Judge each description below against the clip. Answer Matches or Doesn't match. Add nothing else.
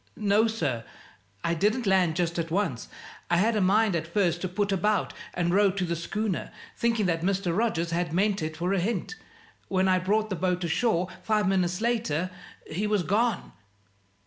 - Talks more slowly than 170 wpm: Doesn't match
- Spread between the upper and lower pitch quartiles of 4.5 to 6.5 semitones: Doesn't match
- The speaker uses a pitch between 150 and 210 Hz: Matches